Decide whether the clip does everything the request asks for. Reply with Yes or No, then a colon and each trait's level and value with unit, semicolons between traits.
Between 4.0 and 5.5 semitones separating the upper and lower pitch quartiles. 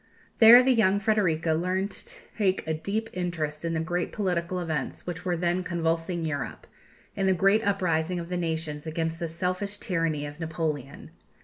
No: average, 2.8 semitones